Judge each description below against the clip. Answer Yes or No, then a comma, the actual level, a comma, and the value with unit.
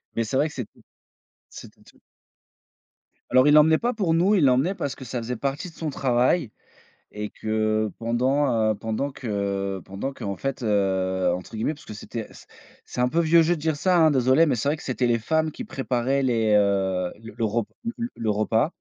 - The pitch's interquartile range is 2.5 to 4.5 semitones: No, wide, 5.6 semitones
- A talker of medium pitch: No, low, 125 Hz